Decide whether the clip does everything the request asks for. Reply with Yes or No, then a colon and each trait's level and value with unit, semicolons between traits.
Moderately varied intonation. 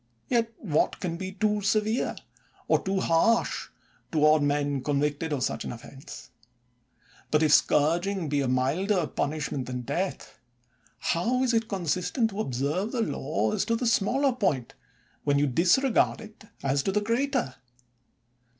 No: wide, 7.0 semitones